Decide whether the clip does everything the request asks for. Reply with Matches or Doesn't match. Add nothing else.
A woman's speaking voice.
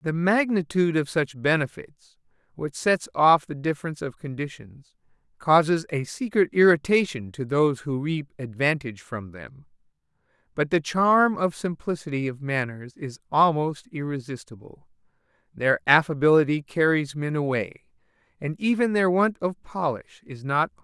Doesn't match